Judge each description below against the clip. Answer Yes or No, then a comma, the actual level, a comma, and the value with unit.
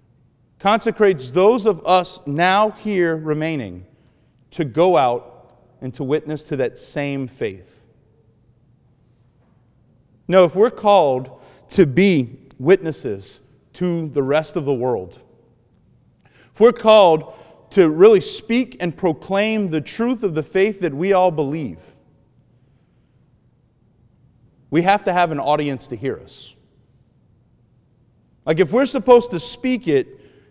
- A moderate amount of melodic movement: No, wide, 7.2 semitones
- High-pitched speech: No, medium, 150 Hz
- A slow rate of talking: Yes, slow, 125 wpm